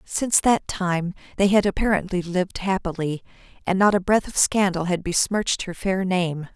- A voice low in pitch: No, medium, 185 Hz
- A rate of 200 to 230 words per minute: No, average, 175 wpm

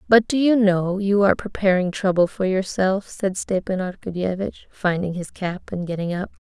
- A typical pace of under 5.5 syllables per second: Yes, 5.0 syllables/s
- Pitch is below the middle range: No, high, 190 Hz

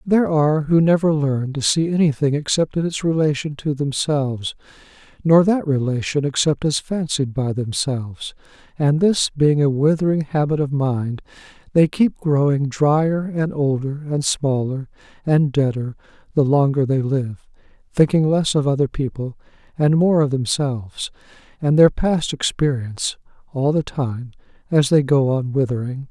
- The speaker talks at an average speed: Yes, average, 145 wpm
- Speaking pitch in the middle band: Yes, medium, 145 Hz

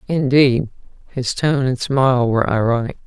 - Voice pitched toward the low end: Yes, low, 130 Hz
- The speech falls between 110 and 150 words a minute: Yes, slow, 135 wpm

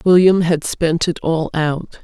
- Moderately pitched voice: Yes, medium, 165 Hz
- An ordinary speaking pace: Yes, average, 175 wpm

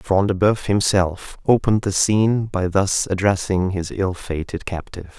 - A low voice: Yes, very low, 95 Hz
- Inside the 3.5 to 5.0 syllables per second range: Yes, 4.6 syllables/s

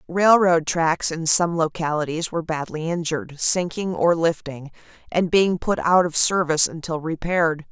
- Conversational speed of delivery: Yes, average, 150 wpm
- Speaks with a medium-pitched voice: Yes, medium, 165 Hz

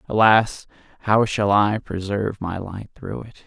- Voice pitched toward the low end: Yes, low, 105 Hz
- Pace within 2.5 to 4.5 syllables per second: Yes, 4.1 syllables/s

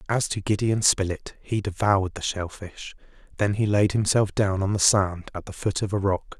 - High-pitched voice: No, low, 100 Hz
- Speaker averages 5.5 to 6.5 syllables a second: No, 4.9 syllables/s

